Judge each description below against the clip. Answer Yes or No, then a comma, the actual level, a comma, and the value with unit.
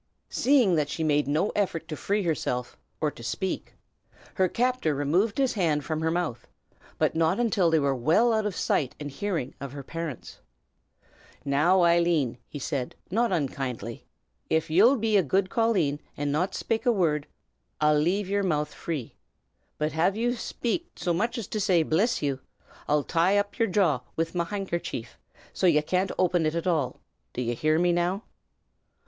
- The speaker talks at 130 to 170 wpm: No, average, 185 wpm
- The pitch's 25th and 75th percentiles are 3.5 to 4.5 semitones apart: No, average, 5.0 semitones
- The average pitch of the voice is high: No, medium, 170 Hz